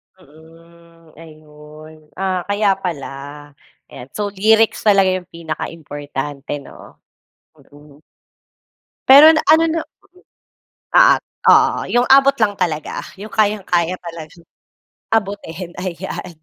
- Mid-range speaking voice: Yes, medium, 175 Hz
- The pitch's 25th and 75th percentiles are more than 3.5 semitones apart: Yes, average, 4.6 semitones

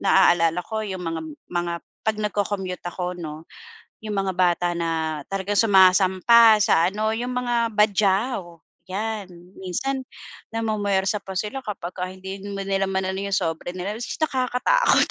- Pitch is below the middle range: No, high, 195 Hz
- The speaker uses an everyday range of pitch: Yes, average, 3.2 semitones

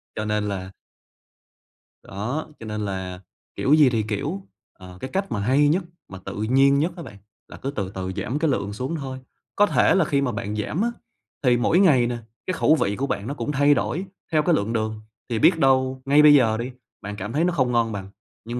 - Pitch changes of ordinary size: No, wide, 5.8 semitones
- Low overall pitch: Yes, low, 125 Hz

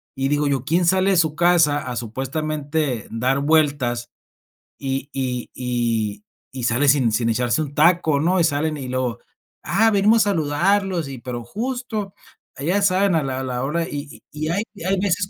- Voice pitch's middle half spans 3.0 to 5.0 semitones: No, wide, 5.4 semitones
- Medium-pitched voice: Yes, medium, 145 Hz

